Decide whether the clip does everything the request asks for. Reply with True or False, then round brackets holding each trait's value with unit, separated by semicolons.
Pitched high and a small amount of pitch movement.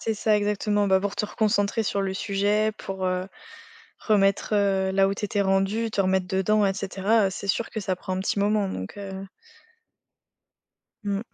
True (200 Hz; 1.5 semitones)